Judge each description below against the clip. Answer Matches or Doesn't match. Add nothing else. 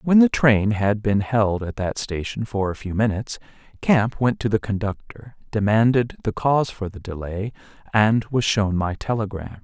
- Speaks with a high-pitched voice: Doesn't match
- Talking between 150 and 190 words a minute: Matches